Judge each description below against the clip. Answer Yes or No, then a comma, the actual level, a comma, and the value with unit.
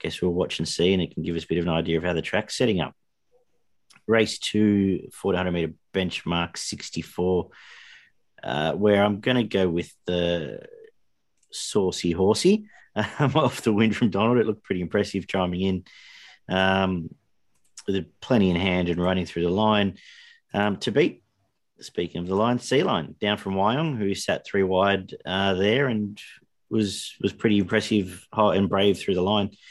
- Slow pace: No, average, 175 wpm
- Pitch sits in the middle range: No, low, 100 Hz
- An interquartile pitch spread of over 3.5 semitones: No, average, 3.1 semitones